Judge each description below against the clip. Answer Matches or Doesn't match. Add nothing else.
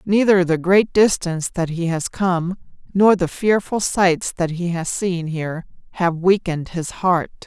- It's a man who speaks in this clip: Doesn't match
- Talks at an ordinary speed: Matches